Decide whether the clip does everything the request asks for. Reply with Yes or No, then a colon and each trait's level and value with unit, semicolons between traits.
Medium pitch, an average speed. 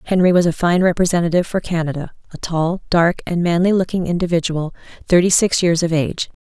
Yes: medium, 170 Hz; average, 175 wpm